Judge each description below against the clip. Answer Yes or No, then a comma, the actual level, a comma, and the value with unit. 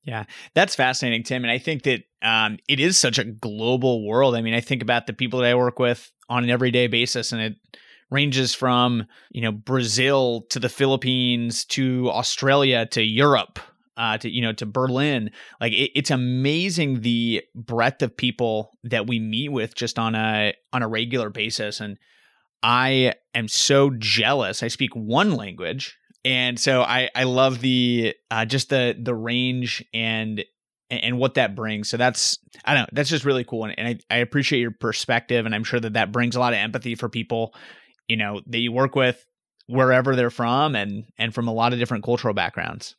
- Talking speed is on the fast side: No, average, 195 wpm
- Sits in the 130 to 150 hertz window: No, low, 120 Hz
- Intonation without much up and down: Yes, narrow, 2.1 semitones